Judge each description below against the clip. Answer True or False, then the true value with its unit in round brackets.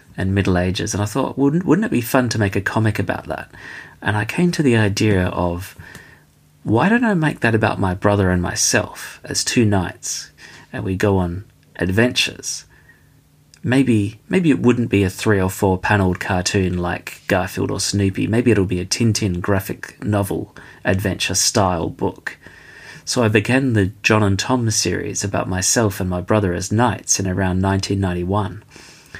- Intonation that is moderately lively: True (4.1 semitones)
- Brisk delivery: False (180 wpm)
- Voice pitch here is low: True (100 Hz)